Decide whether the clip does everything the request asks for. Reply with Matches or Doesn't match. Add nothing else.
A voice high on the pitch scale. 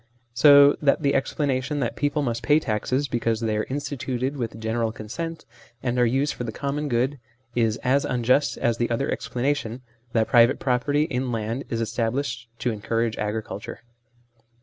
Doesn't match